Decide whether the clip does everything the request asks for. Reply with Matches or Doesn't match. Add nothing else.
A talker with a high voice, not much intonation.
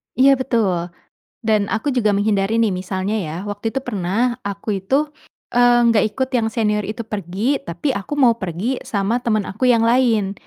Doesn't match